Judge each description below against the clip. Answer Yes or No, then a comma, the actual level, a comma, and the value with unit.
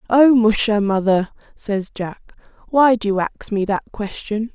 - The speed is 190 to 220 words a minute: No, average, 160 wpm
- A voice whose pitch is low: No, high, 215 Hz